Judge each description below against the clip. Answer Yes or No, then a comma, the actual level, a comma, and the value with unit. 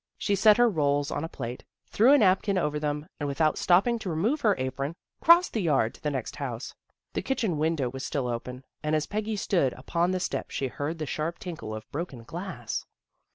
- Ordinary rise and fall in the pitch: No, wide, 5.9 semitones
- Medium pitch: Yes, medium, 155 Hz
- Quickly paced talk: Yes, fast, 210 wpm